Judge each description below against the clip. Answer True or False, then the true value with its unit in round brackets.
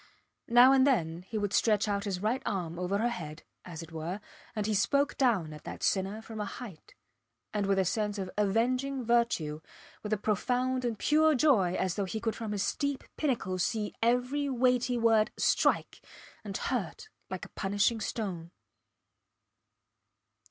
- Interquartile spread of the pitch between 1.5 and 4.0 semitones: False (4.4 semitones)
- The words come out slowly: False (170 wpm)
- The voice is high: True (215 Hz)